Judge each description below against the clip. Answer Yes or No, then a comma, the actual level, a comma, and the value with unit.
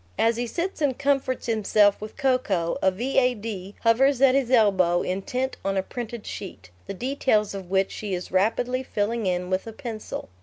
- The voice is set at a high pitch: Yes, high, 220 Hz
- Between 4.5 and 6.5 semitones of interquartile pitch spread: Yes, average, 4.8 semitones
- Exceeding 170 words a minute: Yes, average, 180 wpm